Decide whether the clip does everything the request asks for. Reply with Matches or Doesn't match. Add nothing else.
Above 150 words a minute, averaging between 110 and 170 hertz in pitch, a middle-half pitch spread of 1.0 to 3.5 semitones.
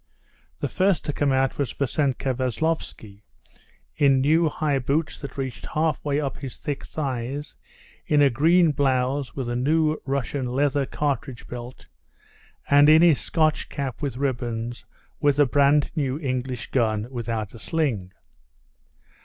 Doesn't match